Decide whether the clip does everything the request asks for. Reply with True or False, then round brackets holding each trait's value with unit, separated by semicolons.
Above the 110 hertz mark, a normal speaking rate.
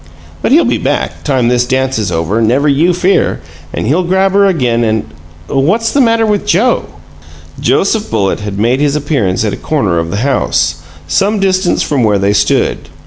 True (135 Hz; 190 wpm)